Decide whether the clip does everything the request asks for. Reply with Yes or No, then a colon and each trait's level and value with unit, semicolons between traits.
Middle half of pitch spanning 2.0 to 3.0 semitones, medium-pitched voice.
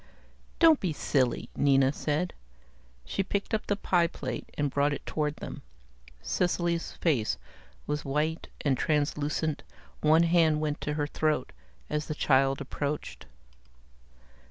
Yes: average, 2.7 semitones; medium, 150 Hz